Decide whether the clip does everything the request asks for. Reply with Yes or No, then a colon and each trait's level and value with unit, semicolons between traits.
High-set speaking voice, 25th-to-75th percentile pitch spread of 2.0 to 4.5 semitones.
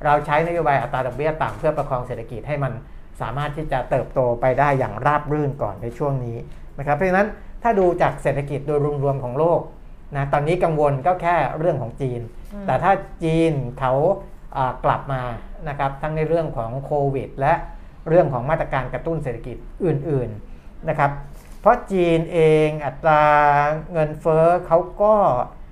No: medium, 145 Hz; average, 3.8 semitones